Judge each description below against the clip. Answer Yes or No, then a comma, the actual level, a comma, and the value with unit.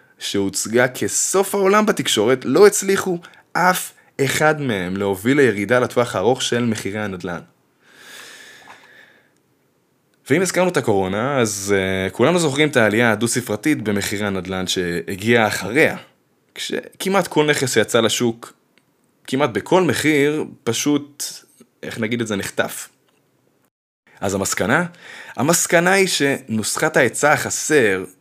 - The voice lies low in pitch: Yes, low, 120 Hz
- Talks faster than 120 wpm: No, average, 110 wpm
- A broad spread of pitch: Yes, wide, 7.0 semitones